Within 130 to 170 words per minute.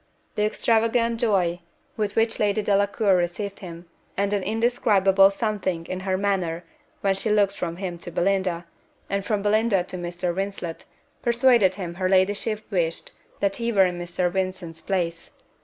Yes: average, 155 wpm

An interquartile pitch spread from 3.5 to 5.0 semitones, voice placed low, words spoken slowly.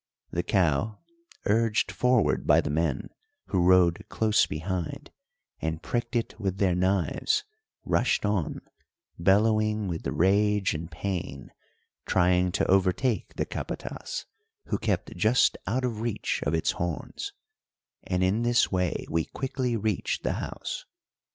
Yes: average, 4.0 semitones; very low, 95 Hz; slow, 130 wpm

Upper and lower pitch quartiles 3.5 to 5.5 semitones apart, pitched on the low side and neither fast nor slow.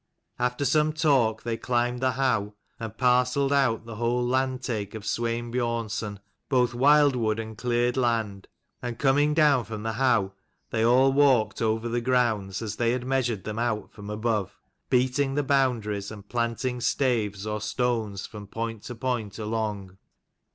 No: average, 2.8 semitones; low, 120 Hz; average, 160 wpm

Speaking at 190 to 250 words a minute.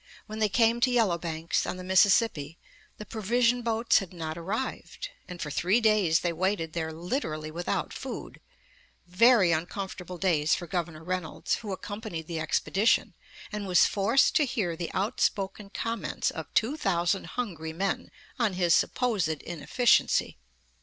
No: average, 150 wpm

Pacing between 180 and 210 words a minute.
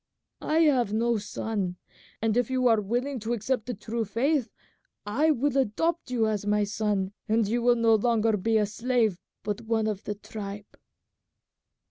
No: average, 170 wpm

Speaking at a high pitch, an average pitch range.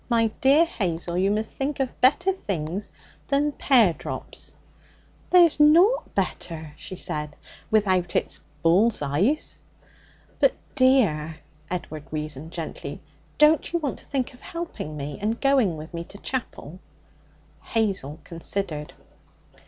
No: high, 200 Hz; wide, 9.0 semitones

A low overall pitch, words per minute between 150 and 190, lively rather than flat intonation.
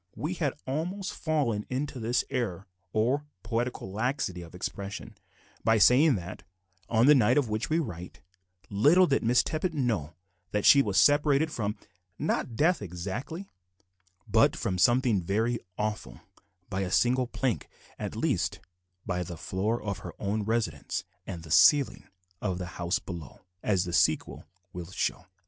Yes: low, 110 Hz; average, 155 wpm; wide, 6.6 semitones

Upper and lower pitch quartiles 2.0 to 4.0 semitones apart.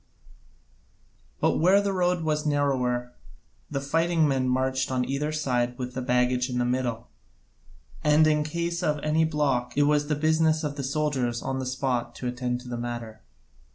Yes: average, 3.6 semitones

